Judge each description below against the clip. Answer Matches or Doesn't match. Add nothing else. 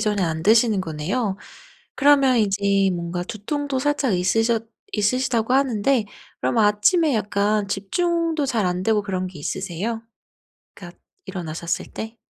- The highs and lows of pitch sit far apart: Doesn't match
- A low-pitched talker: Doesn't match